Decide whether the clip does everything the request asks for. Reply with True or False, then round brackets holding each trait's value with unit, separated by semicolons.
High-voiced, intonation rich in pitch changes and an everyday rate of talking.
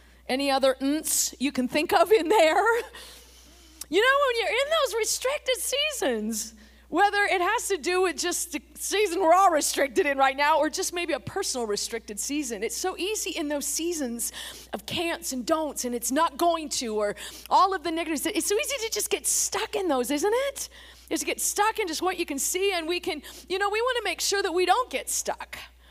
False (335 Hz; 5.8 semitones; 220 wpm)